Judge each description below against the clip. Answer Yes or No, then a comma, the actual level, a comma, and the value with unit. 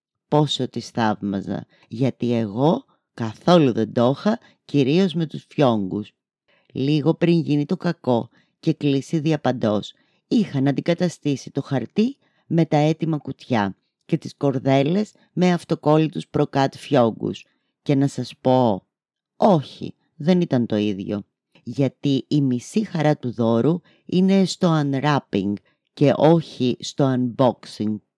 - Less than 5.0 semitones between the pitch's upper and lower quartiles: No, average, 5.3 semitones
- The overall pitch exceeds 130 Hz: Yes, medium, 140 Hz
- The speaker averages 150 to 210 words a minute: No, average, 125 wpm